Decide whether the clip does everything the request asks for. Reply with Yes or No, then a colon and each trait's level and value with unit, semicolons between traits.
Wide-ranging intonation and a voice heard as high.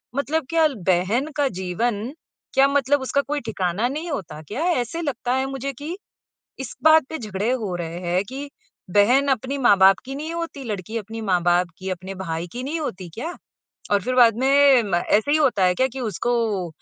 Yes: wide, 6.6 semitones; high, 245 Hz